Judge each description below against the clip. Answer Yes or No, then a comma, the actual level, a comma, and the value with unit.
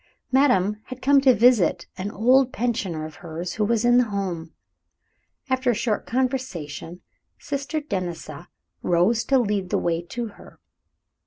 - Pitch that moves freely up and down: Yes, wide, 6.2 semitones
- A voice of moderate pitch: No, high, 215 Hz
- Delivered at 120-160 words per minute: Yes, average, 150 wpm